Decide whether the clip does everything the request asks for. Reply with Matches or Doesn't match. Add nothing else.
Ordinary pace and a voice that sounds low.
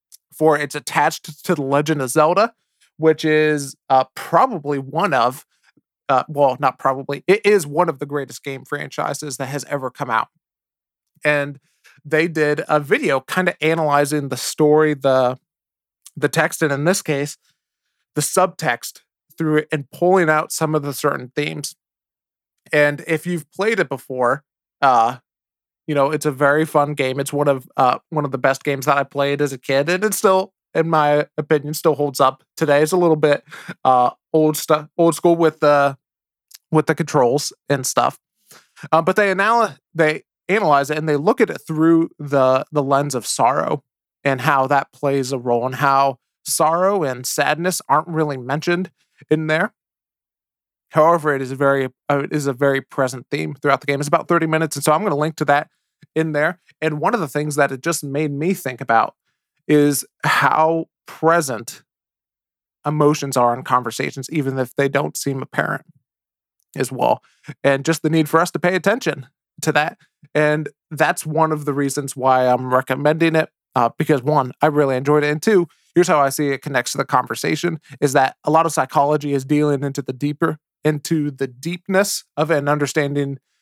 Doesn't match